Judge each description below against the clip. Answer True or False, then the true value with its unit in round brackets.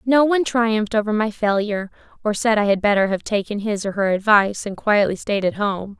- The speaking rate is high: True (220 wpm)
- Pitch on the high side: True (210 Hz)